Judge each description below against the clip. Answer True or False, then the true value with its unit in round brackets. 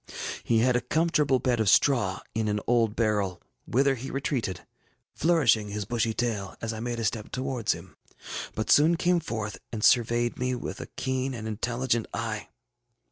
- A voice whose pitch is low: True (120 Hz)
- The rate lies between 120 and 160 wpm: False (175 wpm)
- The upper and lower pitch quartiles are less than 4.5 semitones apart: True (3.3 semitones)